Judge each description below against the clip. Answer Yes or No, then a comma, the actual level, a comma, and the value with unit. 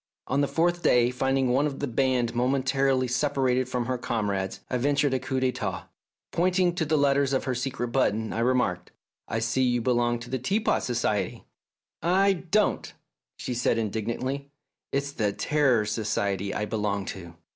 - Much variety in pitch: No, average, 3.2 semitones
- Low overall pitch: Yes, low, 130 Hz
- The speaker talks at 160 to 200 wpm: Yes, average, 180 wpm